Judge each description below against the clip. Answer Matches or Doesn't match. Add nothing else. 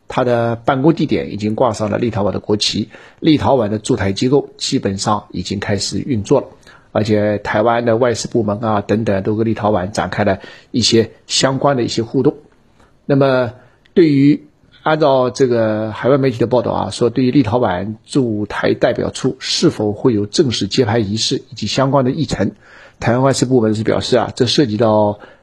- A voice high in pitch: Doesn't match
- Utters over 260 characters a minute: Matches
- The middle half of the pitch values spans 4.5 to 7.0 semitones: Doesn't match